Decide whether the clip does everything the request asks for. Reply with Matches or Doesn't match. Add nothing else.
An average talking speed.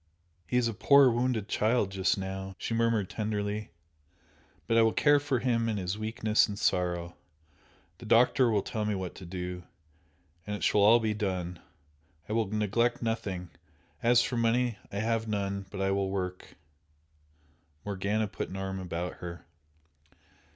Matches